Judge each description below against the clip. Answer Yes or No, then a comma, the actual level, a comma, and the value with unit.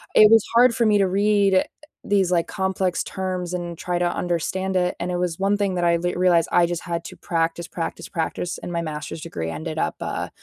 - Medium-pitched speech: Yes, medium, 180 Hz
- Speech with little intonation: Yes, narrow, 2.0 semitones